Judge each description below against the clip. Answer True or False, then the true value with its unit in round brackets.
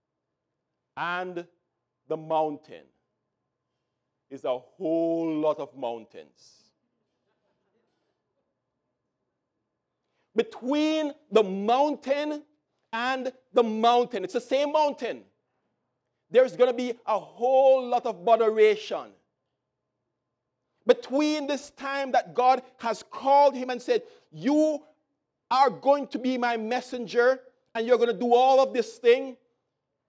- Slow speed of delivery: True (105 wpm)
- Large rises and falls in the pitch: True (6.2 semitones)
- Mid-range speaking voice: False (245 Hz)